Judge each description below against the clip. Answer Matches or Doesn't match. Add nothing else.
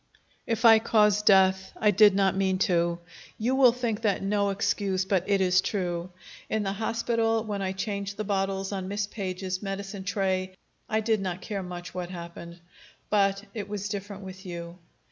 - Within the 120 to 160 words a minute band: Doesn't match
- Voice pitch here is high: Matches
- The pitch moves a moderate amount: Doesn't match